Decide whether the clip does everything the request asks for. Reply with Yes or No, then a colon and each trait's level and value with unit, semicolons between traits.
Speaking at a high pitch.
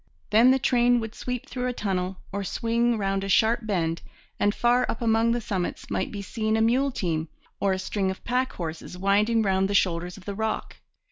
Yes: high, 210 Hz